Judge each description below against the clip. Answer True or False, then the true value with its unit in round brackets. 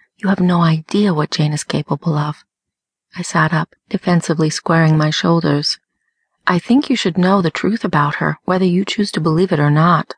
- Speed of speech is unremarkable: True (195 wpm)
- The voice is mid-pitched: True (175 Hz)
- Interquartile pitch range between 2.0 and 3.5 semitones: False (3.9 semitones)